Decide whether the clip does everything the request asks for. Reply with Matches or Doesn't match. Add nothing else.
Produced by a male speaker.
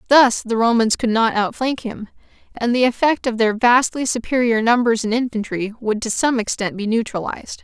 Doesn't match